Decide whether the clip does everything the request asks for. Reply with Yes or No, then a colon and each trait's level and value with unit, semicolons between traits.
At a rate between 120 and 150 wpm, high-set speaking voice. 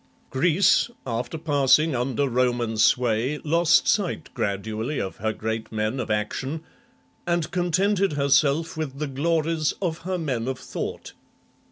No: slow, 135 wpm; medium, 140 Hz